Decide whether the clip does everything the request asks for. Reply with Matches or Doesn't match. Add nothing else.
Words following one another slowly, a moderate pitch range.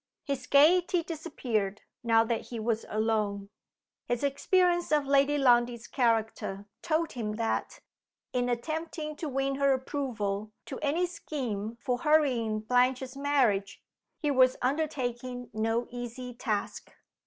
Matches